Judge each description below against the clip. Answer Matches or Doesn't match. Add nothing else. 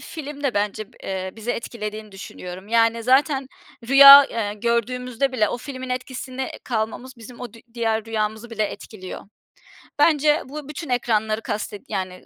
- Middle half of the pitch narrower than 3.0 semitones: Doesn't match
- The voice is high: Matches